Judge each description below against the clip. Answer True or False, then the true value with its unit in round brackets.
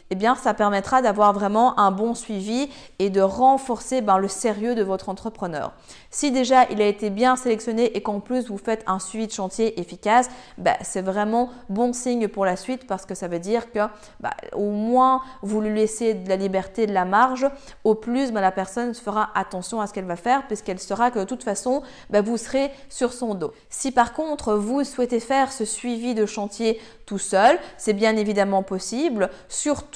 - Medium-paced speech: True (205 wpm)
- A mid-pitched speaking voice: False (220 Hz)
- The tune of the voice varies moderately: True (3.7 semitones)